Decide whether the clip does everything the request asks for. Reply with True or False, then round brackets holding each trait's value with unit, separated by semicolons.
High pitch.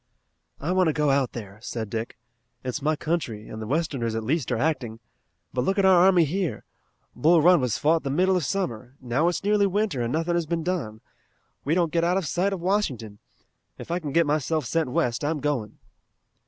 False (155 Hz)